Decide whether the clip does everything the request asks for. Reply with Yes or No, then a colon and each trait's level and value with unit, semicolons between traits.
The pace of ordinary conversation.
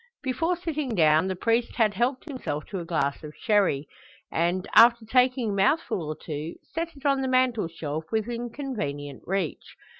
Yes: average, 170 wpm